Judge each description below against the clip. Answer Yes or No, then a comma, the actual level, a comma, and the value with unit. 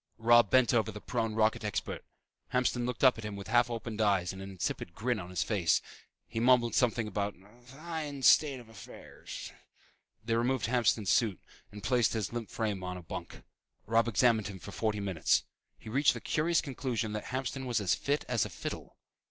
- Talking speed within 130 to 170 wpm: No, average, 195 wpm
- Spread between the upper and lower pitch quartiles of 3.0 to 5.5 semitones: Yes, average, 3.3 semitones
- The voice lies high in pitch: No, low, 115 Hz